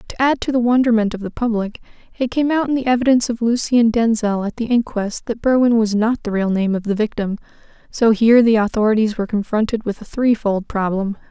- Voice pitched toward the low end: No, high, 225 Hz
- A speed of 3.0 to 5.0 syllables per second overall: No, 6.0 syllables/s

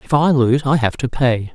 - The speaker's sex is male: Yes, male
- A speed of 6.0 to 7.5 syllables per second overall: No, 5.0 syllables/s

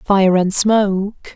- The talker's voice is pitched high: Yes, high, 195 Hz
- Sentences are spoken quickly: No, slow, 135 wpm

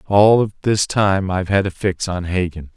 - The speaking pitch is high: No, very low, 95 Hz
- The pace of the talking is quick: Yes, fast, 215 wpm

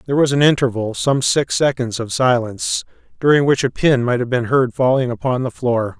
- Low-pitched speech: Yes, low, 125 Hz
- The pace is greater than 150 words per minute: Yes, average, 190 wpm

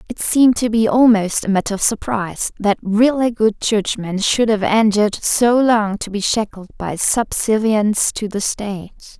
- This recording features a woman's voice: Yes, female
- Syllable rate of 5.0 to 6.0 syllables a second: No, 4.6 syllables/s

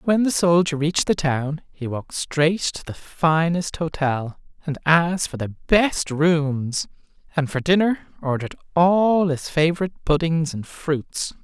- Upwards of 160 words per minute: No, average, 150 wpm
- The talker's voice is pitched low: No, medium, 160 Hz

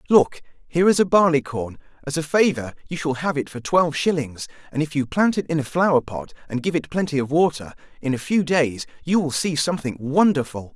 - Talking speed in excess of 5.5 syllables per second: Yes, 5.8 syllables/s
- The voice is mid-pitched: Yes, medium, 150 Hz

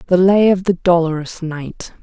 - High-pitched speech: No, medium, 175 Hz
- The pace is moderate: Yes, average, 180 wpm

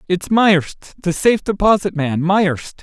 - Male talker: Yes, male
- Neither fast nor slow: No, slow, 130 wpm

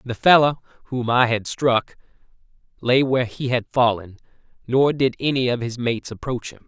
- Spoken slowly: No, average, 170 wpm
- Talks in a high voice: No, low, 125 Hz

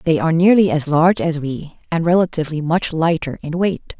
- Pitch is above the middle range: No, medium, 165 Hz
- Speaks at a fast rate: No, average, 195 wpm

